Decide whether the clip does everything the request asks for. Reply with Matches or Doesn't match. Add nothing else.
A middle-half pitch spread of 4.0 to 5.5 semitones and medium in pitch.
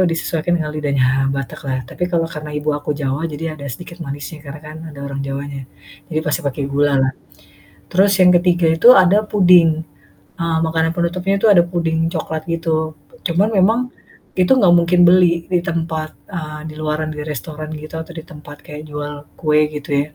Doesn't match